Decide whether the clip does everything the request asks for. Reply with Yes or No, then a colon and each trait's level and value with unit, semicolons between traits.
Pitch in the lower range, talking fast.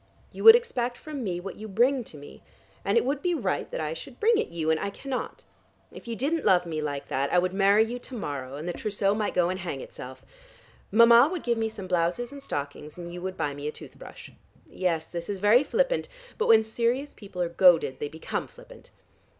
No: high, 195 Hz; fast, 230 wpm